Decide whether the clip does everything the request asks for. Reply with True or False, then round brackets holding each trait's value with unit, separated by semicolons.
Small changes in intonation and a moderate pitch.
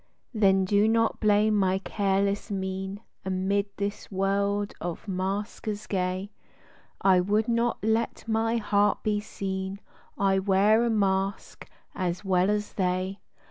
False (1.6 semitones; 200 Hz)